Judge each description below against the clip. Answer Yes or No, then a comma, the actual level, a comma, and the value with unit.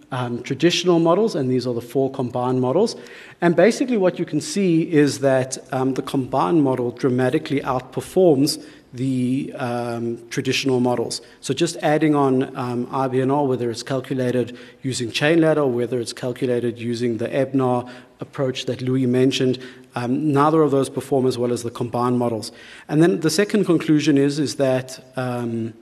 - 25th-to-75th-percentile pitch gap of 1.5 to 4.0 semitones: Yes, average, 2.9 semitones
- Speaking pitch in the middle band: No, low, 130 Hz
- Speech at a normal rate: Yes, average, 165 wpm